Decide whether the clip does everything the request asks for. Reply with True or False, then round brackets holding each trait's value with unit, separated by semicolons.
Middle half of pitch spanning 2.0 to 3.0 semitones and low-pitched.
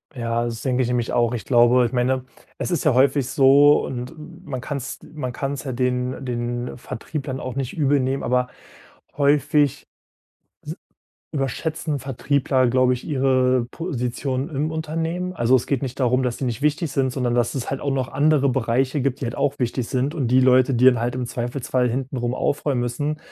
True (2.4 semitones; 130 Hz)